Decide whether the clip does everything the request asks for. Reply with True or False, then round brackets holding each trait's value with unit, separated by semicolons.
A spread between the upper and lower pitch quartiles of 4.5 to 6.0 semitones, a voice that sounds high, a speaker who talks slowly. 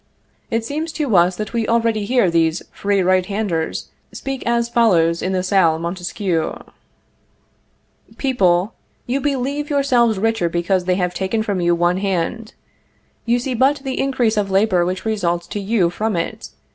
False (4.9 semitones; 205 Hz; 160 wpm)